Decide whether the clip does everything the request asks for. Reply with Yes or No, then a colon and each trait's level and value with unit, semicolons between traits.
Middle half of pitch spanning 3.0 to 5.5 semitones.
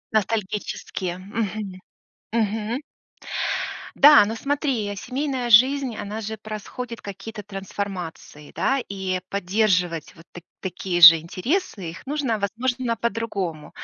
Yes: average, 3.9 semitones